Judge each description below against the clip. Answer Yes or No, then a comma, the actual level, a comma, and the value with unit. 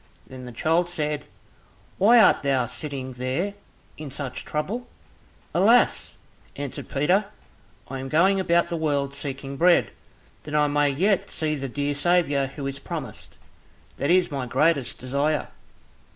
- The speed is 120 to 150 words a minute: Yes, average, 145 wpm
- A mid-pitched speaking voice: Yes, medium, 145 Hz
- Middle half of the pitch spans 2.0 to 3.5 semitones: No, average, 3.9 semitones